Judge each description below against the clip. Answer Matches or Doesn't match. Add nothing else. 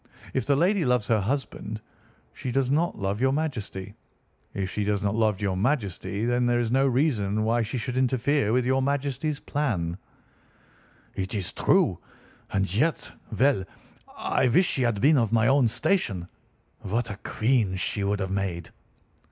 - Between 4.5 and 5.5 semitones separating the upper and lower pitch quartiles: Matches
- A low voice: Matches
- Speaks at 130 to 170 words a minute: Matches